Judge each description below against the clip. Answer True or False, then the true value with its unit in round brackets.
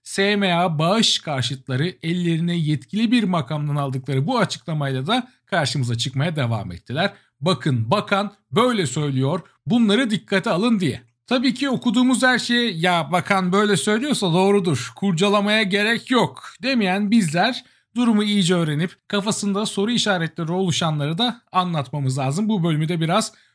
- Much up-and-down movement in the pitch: True (5.8 semitones)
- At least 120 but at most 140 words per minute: True (135 wpm)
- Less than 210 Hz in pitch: True (185 Hz)